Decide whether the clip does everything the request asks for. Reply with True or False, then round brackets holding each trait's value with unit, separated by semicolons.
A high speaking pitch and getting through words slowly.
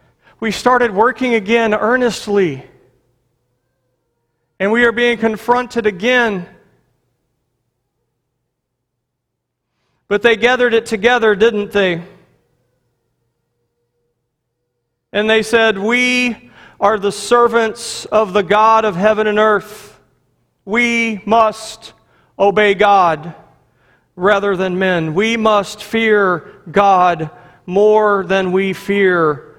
True (200 Hz; 95 wpm)